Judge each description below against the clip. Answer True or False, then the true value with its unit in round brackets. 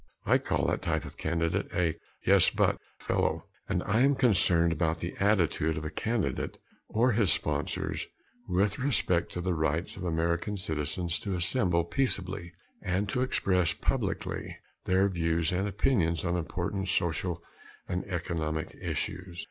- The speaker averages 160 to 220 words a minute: False (150 wpm)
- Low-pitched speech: True (90 Hz)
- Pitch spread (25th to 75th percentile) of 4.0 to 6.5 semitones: False (3.0 semitones)